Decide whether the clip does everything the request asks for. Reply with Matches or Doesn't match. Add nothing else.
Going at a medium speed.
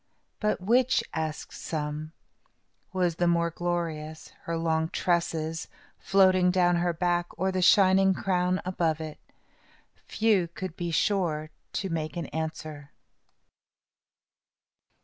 Doesn't match